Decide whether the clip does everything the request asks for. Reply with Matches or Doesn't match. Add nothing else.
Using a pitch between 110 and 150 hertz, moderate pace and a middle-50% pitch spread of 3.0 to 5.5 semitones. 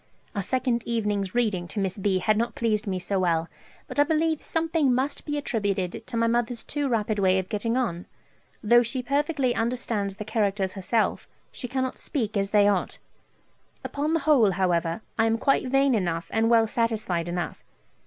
Doesn't match